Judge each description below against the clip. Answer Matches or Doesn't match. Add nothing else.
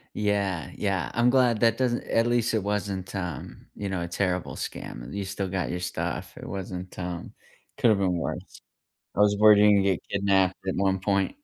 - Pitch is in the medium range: Doesn't match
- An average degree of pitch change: Doesn't match